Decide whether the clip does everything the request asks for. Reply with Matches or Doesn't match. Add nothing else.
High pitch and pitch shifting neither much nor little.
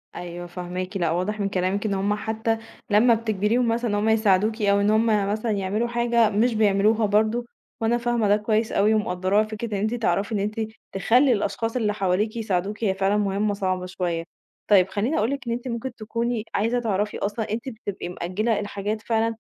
Doesn't match